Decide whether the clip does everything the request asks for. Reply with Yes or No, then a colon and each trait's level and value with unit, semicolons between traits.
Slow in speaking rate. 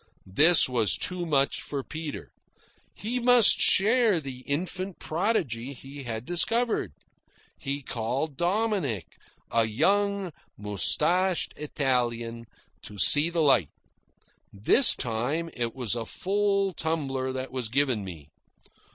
Yes: slow, 115 wpm